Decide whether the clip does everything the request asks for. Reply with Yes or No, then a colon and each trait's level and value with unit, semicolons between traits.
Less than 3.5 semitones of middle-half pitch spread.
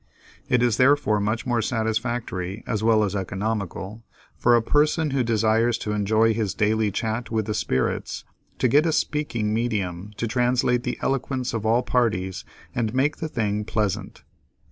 Yes: narrow, 2.6 semitones